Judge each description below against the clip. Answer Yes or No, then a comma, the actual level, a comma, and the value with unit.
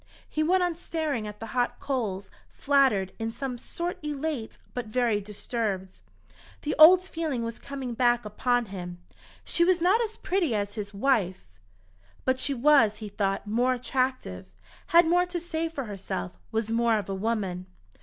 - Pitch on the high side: Yes, high, 245 Hz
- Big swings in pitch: Yes, wide, 6.6 semitones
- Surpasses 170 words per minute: No, average, 165 wpm